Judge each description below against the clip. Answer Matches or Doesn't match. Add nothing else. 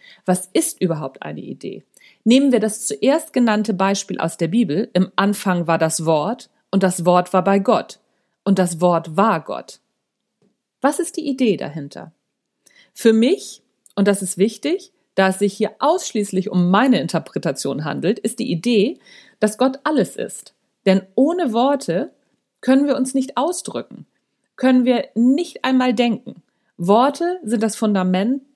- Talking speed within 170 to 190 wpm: Doesn't match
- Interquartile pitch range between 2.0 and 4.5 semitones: Doesn't match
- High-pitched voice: Matches